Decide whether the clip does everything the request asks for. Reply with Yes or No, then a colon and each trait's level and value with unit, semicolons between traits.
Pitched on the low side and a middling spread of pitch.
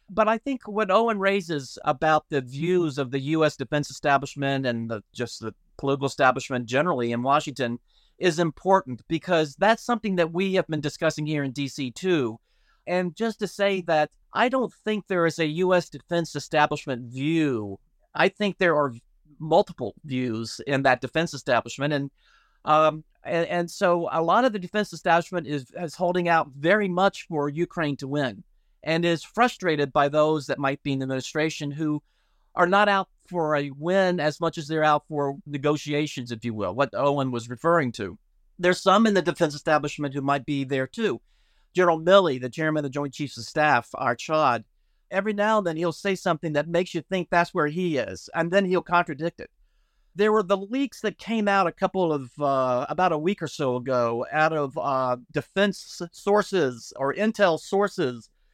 No: medium, 155 Hz; average, 4.5 semitones